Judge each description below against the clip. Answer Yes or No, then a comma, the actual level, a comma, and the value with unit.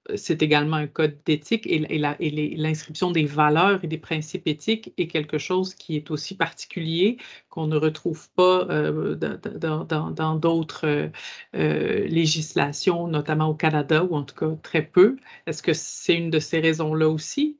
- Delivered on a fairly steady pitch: Yes, narrow, 1.9 semitones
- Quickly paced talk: No, average, 150 wpm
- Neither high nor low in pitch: Yes, medium, 155 Hz